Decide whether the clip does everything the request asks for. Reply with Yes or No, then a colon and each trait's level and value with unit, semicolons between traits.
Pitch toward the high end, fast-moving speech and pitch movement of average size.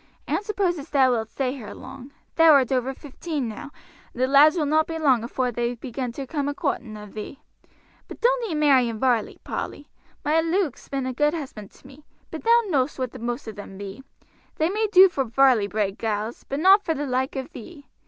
Yes: very high, 270 Hz; fast, 225 wpm; average, 4.5 semitones